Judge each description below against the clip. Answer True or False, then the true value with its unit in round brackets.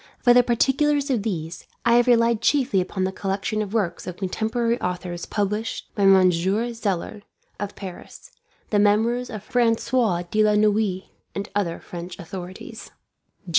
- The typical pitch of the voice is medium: False (210 Hz)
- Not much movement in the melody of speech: False (3.8 semitones)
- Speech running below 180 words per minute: True (150 wpm)